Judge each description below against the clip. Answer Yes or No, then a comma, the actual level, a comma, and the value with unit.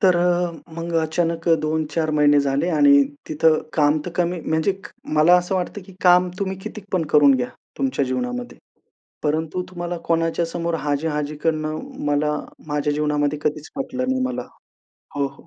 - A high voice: No, medium, 160 Hz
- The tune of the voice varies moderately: Yes, average, 3.1 semitones